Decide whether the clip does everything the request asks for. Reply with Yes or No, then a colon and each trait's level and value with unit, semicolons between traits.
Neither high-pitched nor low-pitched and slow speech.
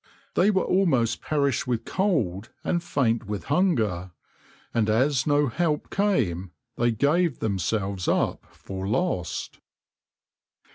No: low, 120 Hz; slow, 115 wpm